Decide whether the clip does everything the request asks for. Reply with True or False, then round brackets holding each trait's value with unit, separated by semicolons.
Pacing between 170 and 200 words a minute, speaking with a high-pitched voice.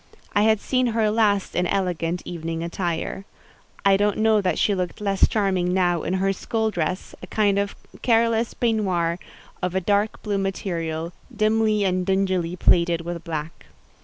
False (160 wpm; 195 Hz)